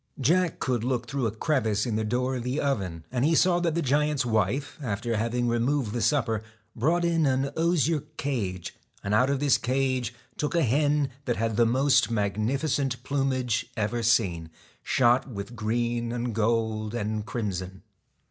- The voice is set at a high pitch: No, low, 120 Hz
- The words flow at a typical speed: Yes, average, 185 wpm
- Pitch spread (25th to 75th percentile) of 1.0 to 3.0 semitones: No, average, 3.9 semitones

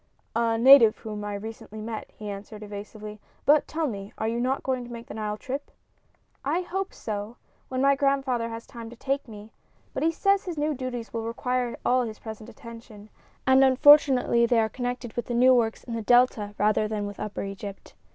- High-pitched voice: Yes, high, 235 Hz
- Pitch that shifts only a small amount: No, average, 3.4 semitones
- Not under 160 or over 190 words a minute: No, average, 200 wpm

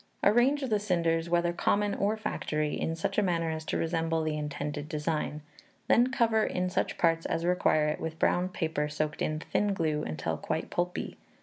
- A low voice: No, medium, 165 Hz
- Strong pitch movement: No, average, 3.9 semitones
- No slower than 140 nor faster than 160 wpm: No, average, 185 wpm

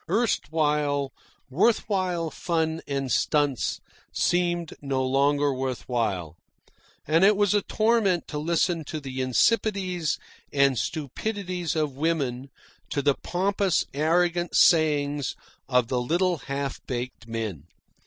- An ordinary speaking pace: No, slow, 120 wpm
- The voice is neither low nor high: Yes, medium, 150 Hz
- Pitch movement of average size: Yes, average, 4.7 semitones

